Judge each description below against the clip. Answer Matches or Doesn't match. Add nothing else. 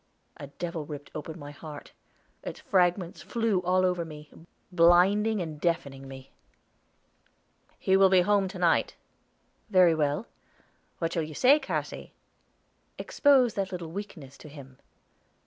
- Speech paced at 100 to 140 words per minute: Matches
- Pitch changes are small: Doesn't match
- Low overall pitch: Doesn't match